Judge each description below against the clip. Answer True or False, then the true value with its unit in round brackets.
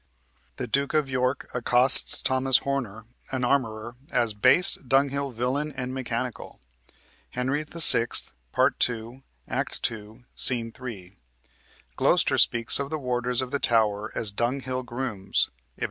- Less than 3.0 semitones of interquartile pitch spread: True (2.6 semitones)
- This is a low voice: True (125 Hz)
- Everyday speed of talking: False (130 wpm)